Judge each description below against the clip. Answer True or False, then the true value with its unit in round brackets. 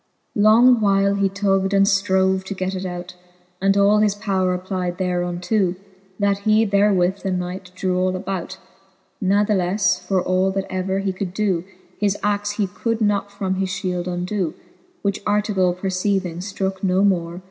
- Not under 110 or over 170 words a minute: True (165 wpm)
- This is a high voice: True (195 Hz)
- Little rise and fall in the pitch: True (1.7 semitones)